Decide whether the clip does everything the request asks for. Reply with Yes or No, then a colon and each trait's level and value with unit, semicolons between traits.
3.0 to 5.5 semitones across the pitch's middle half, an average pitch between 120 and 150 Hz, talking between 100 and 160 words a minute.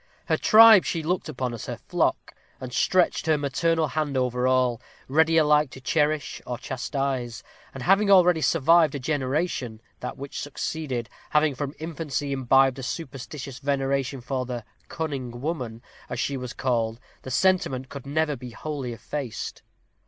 Yes: average, 3.6 semitones; medium, 140 Hz; average, 155 wpm